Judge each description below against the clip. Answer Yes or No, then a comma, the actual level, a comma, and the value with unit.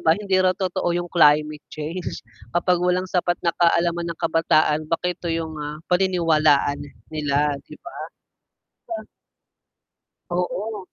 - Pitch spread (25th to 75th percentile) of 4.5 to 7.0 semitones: No, average, 2.7 semitones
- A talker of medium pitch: Yes, medium, 170 Hz